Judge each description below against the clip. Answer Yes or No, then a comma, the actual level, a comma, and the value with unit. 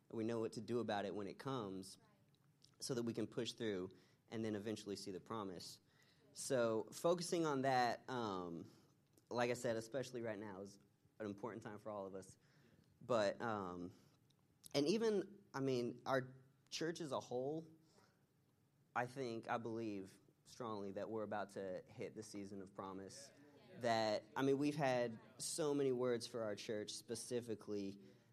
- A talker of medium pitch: No, low, 115 Hz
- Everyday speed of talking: Yes, average, 165 wpm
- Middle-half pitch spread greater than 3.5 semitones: Yes, average, 4.7 semitones